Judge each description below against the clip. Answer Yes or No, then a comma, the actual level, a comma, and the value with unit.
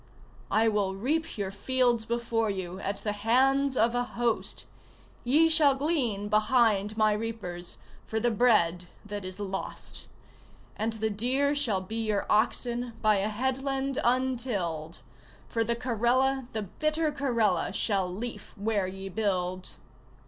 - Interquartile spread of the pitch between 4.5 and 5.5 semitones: No, average, 4.0 semitones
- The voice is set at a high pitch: Yes, high, 225 Hz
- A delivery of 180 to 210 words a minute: No, average, 140 wpm